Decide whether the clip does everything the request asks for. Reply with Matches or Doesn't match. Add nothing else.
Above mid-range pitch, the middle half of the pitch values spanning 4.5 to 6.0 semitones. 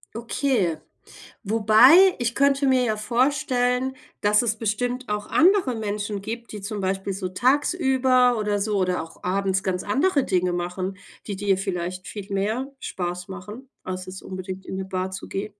Matches